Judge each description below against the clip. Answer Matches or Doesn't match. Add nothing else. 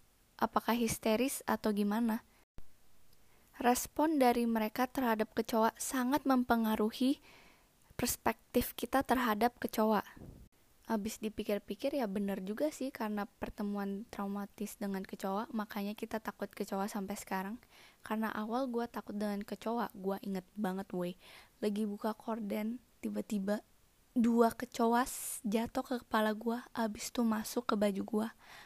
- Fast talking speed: Doesn't match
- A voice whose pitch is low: Doesn't match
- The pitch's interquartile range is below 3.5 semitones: Matches